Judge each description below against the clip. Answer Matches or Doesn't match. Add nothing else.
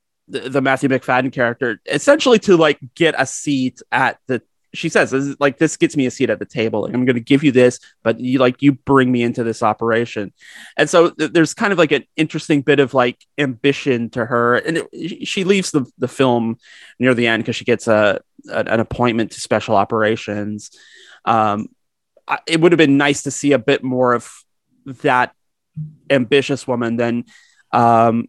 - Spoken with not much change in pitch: Doesn't match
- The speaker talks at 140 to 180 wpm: Doesn't match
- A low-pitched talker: Matches